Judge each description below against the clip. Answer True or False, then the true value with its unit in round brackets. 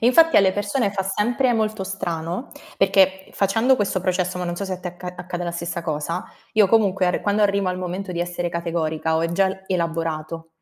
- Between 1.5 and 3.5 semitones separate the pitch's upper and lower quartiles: True (2.6 semitones)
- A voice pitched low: False (185 Hz)